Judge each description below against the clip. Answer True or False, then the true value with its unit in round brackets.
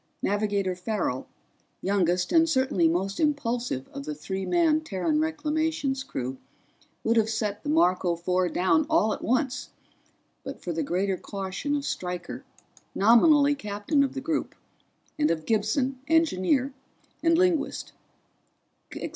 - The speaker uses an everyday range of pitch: False (8.1 semitones)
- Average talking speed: False (130 wpm)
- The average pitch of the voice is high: True (225 Hz)